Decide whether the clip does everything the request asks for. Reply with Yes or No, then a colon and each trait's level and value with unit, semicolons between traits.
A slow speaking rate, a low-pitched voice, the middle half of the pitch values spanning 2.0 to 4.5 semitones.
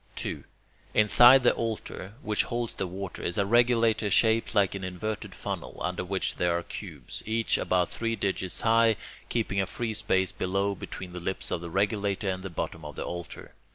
No: average, 190 wpm; low, 100 Hz; average, 3.4 semitones